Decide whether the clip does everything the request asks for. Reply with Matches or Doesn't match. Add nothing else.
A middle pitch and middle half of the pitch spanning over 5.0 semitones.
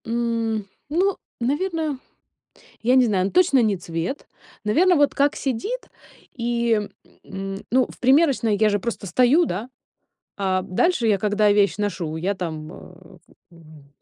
Doesn't match